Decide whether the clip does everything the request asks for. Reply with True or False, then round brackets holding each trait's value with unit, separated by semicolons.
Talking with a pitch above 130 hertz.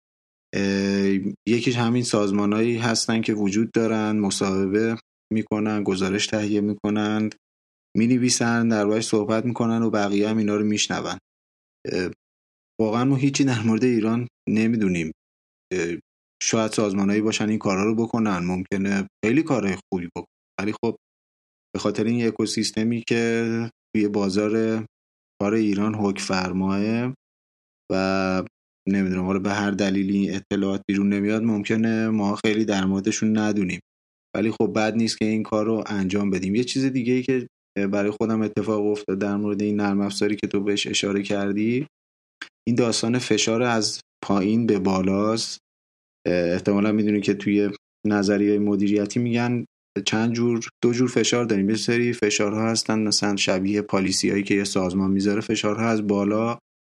False (105 Hz)